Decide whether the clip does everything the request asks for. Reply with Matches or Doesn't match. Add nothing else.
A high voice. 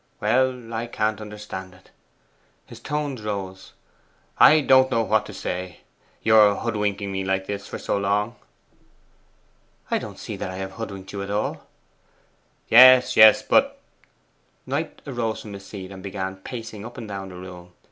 Doesn't match